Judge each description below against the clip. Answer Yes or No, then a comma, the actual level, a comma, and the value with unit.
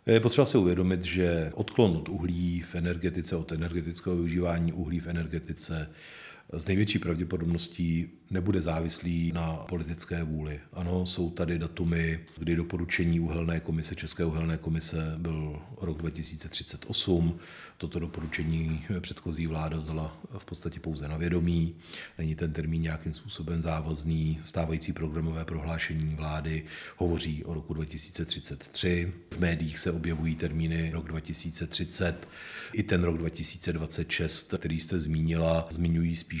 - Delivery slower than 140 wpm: Yes, average, 130 wpm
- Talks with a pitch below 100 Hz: Yes, very low, 85 Hz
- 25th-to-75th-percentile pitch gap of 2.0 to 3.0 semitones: No, narrow, 1.3 semitones